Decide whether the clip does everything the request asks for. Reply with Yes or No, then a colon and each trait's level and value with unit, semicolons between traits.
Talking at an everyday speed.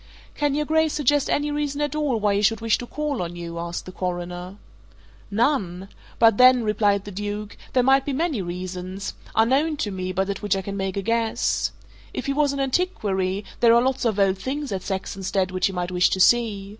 No: fast, 215 wpm